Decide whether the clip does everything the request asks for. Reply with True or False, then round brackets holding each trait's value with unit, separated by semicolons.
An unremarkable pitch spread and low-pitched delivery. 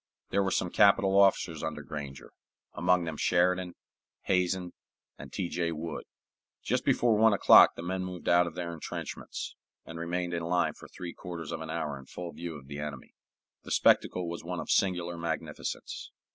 False (1.8 semitones; 85 Hz)